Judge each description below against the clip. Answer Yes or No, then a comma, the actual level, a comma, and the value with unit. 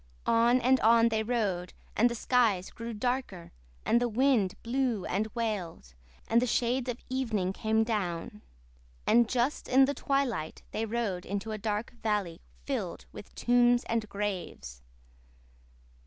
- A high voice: Yes, high, 225 Hz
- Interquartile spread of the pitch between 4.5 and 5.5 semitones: No, average, 3.2 semitones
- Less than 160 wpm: Yes, average, 145 wpm